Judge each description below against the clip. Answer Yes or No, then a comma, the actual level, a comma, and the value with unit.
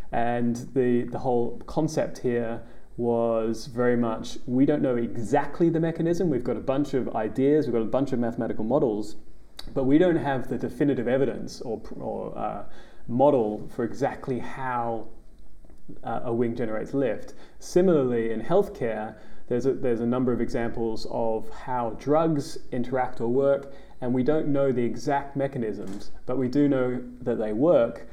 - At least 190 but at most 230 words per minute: No, average, 165 wpm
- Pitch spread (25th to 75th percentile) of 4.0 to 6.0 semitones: No, average, 3.1 semitones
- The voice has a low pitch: Yes, low, 120 Hz